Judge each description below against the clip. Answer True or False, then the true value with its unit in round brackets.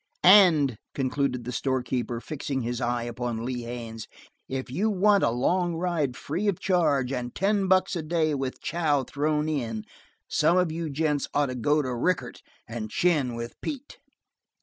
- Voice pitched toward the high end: False (140 Hz)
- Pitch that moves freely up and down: True (5.7 semitones)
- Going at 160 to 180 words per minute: True (170 wpm)